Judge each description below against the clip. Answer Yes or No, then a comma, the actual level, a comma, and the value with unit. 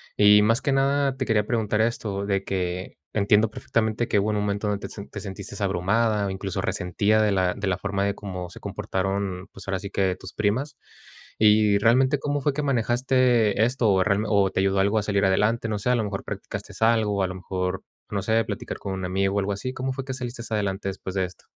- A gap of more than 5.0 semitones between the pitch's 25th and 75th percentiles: No, average, 2.9 semitones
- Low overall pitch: Yes, low, 105 Hz